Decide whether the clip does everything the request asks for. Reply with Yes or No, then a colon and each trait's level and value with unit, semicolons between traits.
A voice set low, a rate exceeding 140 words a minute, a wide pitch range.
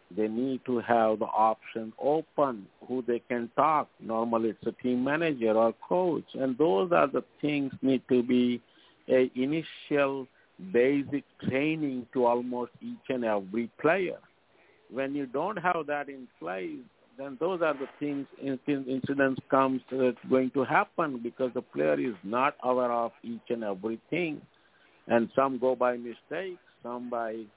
No: low, 130 Hz; average, 155 wpm; average, 3.1 semitones